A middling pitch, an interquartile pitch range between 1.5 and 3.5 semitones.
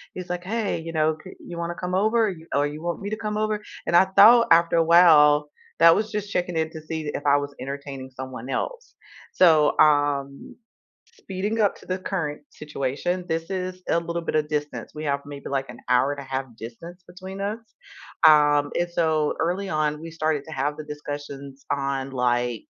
No: medium, 160 Hz; average, 4.0 semitones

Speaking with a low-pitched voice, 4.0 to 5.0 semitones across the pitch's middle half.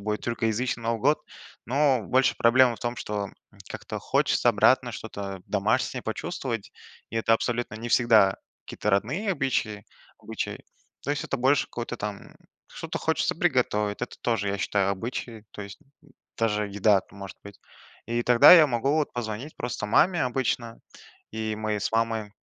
No: low, 115 Hz; average, 2.9 semitones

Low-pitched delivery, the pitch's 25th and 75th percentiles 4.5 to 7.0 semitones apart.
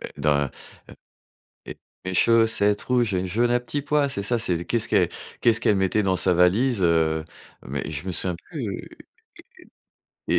Yes: low, 100 Hz; average, 4.9 semitones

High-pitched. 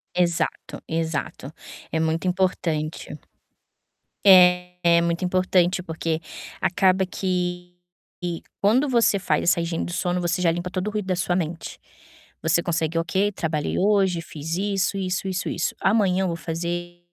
No: medium, 180 Hz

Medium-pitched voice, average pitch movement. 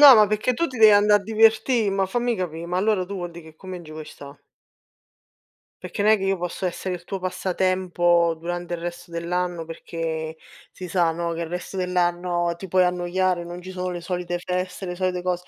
No: medium, 180 Hz; narrow, 1.7 semitones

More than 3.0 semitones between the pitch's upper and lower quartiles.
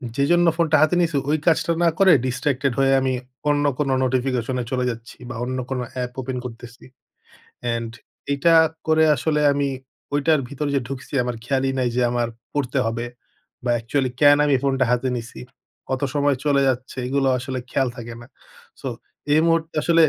No: average, 2.7 semitones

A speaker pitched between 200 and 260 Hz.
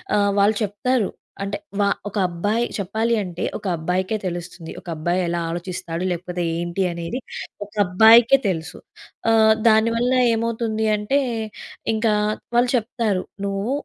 Yes: high, 205 Hz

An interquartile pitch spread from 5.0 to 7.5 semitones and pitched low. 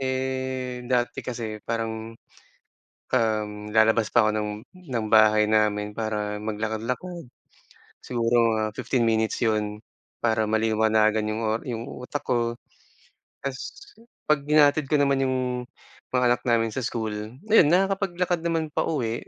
No: average, 3.1 semitones; low, 115 Hz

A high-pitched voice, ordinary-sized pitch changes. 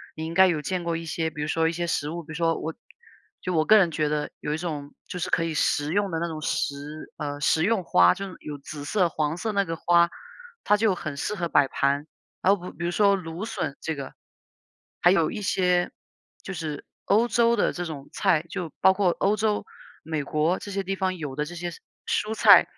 No: medium, 170 Hz; average, 3.7 semitones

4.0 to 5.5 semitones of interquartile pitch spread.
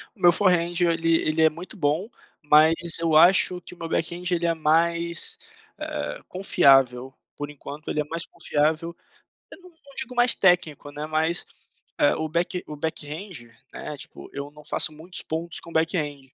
No: narrow, 2.6 semitones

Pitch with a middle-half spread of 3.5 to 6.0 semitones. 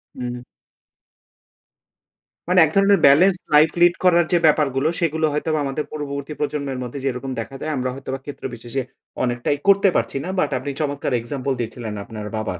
Yes: average, 3.8 semitones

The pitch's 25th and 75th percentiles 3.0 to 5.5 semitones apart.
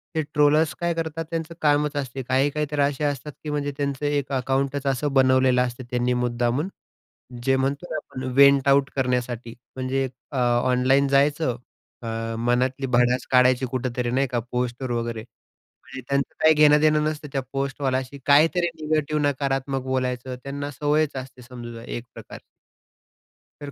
No: narrow, 2.5 semitones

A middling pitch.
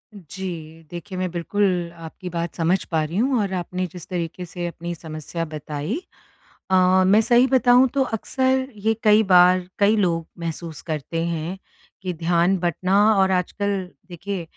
Yes: medium, 180 Hz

